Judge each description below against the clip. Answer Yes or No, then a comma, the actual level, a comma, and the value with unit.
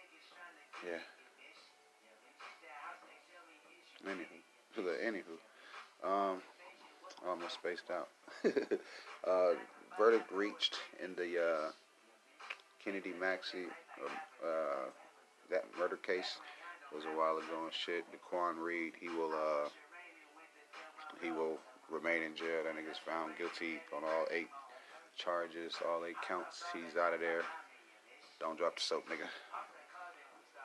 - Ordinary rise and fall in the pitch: No, narrow, 1.5 semitones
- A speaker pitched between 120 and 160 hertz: No, very low, 85 Hz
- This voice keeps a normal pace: No, slow, 115 wpm